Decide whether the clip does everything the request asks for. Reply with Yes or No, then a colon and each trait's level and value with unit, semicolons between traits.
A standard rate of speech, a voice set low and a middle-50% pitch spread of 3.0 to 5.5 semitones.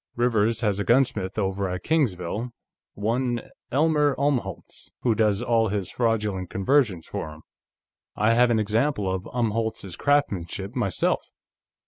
No: slow, 130 wpm; low, 110 Hz; average, 4.0 semitones